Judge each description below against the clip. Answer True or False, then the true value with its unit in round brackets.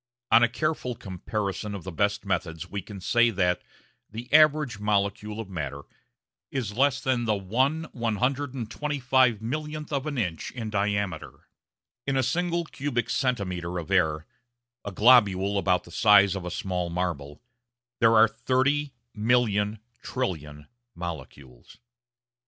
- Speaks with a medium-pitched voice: False (105 Hz)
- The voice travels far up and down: True (5.7 semitones)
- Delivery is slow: True (130 wpm)